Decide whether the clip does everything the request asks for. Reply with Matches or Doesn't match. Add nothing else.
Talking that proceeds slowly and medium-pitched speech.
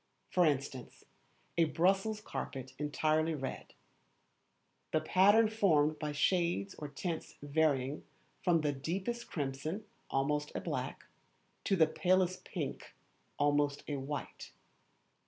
Matches